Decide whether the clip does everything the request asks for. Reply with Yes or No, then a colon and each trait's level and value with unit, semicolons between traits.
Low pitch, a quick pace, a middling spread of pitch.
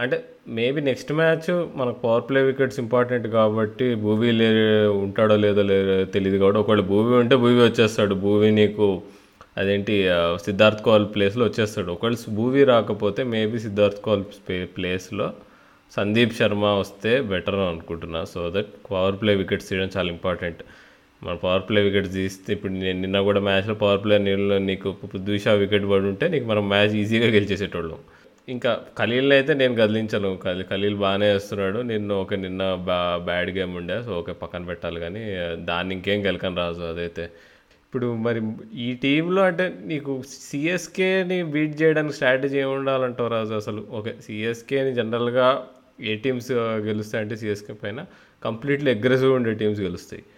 Yes: low, 105 Hz; fast, 150 wpm; average, 3.7 semitones